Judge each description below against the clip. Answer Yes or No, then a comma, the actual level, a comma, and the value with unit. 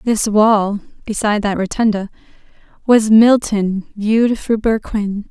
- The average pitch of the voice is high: Yes, high, 210 Hz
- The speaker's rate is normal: No, slow, 115 wpm